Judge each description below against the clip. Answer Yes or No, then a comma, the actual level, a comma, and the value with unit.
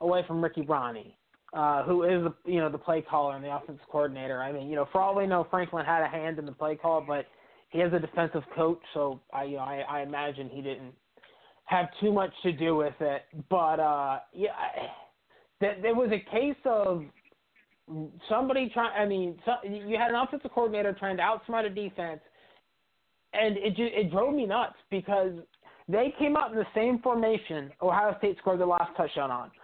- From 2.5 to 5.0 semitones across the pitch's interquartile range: No, wide, 5.4 semitones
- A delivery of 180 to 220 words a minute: Yes, fast, 205 wpm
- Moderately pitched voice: Yes, medium, 175 Hz